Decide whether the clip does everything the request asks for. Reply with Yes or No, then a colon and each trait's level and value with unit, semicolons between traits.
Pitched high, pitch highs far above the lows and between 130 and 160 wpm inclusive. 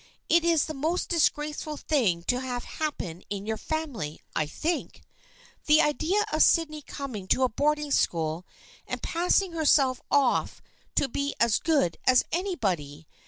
Yes: very high, 280 Hz; wide, 6.9 semitones; average, 150 wpm